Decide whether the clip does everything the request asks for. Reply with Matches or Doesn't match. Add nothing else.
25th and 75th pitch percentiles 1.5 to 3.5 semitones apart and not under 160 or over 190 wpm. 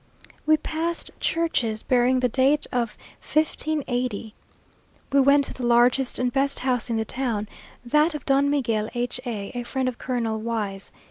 Matches